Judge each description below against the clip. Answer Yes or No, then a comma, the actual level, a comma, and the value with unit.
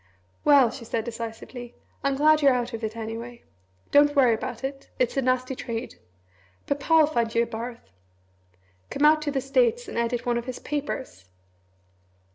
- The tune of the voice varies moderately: Yes, average, 3.5 semitones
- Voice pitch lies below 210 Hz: No, very high, 250 Hz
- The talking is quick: No, average, 170 wpm